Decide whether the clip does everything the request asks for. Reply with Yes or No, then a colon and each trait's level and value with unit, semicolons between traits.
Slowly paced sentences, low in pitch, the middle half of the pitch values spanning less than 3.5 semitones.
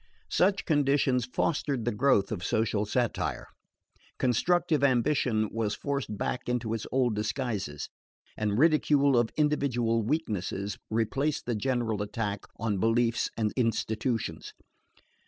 No: slow, 120 wpm; low, 120 Hz; average, 4.3 semitones